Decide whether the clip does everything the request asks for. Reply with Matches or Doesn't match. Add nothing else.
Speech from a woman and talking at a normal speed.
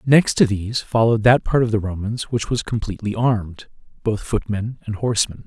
Doesn't match